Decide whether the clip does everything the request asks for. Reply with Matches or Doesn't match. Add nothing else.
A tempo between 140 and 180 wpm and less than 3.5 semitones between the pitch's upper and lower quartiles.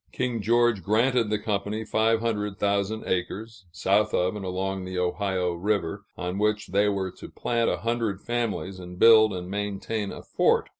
Matches